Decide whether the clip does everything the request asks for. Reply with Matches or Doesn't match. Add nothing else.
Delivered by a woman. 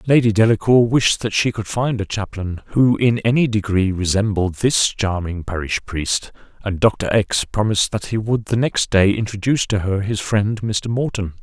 Doesn't match